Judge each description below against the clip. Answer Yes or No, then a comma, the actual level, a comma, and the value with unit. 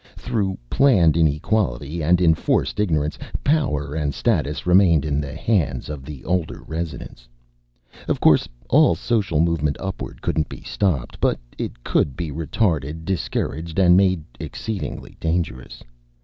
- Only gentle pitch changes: No, average, 4.0 semitones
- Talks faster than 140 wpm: No, slow, 135 wpm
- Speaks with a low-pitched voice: Yes, very low, 80 Hz